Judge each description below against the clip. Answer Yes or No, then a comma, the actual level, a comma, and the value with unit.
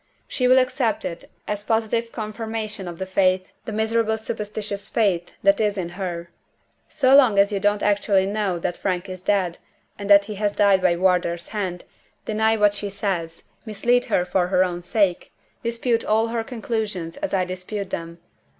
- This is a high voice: Yes, high, 205 Hz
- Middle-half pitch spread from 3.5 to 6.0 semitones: No, average, 3.1 semitones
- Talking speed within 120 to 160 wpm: No, average, 175 wpm